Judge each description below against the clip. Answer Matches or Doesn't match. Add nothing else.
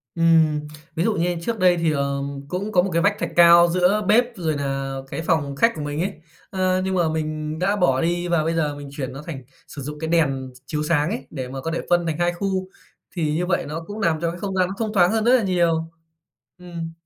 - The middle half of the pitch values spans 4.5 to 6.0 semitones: Doesn't match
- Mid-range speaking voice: Matches